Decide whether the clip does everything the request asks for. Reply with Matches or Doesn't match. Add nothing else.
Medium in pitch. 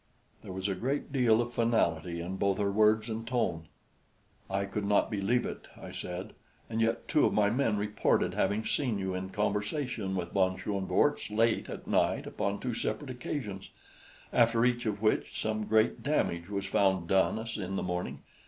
Doesn't match